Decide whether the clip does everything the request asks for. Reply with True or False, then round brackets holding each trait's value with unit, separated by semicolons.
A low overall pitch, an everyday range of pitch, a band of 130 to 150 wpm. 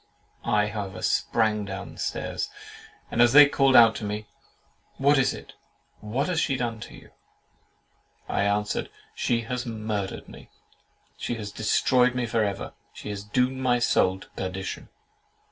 True (110 Hz; 3.4 semitones; 145 wpm)